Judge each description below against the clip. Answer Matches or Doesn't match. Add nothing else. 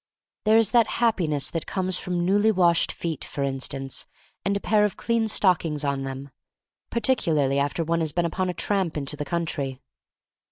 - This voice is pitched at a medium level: Matches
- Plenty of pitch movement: Matches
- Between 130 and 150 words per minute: Doesn't match